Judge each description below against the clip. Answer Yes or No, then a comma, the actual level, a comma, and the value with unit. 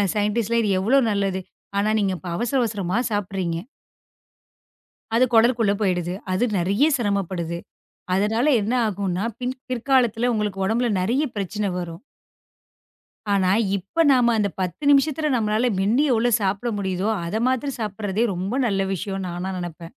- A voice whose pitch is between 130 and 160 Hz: No, high, 205 Hz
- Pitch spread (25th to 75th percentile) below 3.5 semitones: No, average, 3.8 semitones